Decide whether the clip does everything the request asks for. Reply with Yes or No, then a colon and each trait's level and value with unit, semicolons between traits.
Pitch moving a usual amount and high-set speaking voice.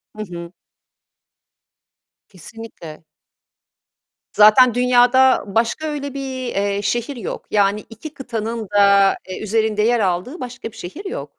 Yes: average, 3.9 semitones; high, 225 Hz